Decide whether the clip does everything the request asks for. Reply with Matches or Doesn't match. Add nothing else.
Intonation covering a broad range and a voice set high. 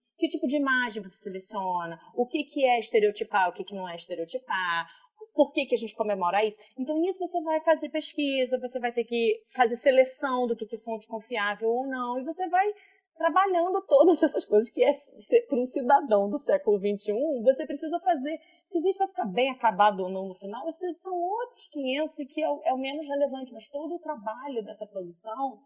Matches